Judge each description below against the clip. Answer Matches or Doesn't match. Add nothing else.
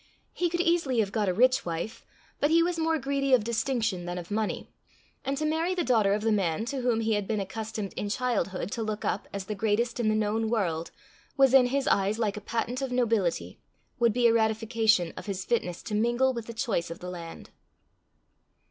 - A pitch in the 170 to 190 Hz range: Doesn't match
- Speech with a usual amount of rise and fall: Matches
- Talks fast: Matches